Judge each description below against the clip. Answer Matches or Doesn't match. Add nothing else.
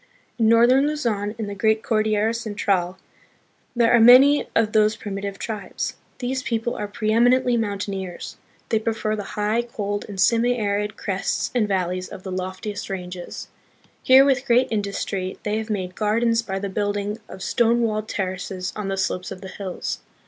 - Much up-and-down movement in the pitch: Doesn't match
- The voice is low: Doesn't match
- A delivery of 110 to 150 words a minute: Doesn't match